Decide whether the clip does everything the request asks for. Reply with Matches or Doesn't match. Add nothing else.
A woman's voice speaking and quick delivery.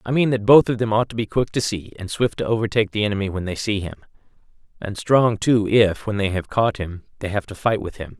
Doesn't match